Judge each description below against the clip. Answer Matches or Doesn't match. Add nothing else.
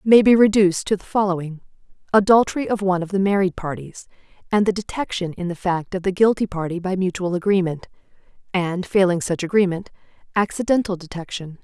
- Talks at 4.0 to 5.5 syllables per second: Doesn't match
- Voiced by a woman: Matches